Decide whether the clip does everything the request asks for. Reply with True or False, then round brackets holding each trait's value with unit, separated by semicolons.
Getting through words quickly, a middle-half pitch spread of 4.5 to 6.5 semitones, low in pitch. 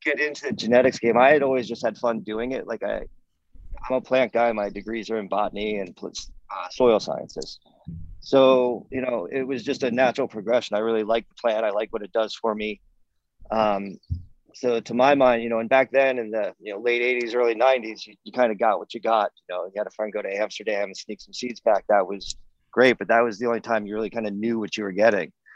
False (250 wpm; 3.2 semitones; 115 Hz)